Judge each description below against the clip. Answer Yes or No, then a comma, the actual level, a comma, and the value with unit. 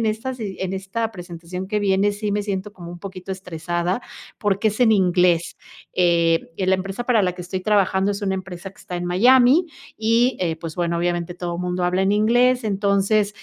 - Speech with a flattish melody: No, average, 3.0 semitones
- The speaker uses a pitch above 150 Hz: Yes, high, 190 Hz